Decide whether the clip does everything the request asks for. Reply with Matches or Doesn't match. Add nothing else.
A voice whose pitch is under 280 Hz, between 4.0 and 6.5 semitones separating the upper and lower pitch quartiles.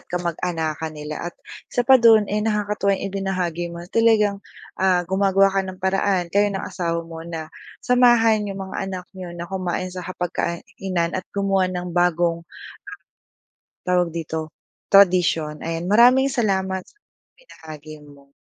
Doesn't match